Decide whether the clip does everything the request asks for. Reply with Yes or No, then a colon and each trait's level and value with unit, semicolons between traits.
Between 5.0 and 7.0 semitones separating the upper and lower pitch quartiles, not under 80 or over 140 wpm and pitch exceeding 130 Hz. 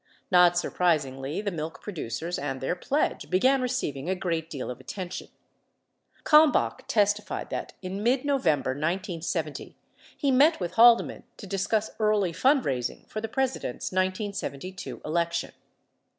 Yes: average, 5.3 semitones; slow, 135 wpm; medium, 185 Hz